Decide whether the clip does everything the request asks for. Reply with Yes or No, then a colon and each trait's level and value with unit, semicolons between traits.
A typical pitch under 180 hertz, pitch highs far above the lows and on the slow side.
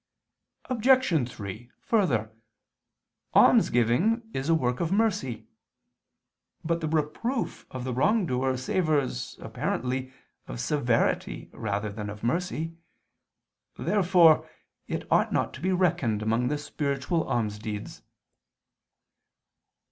Yes: medium, 140 Hz; wide, 7.0 semitones; slow, 105 wpm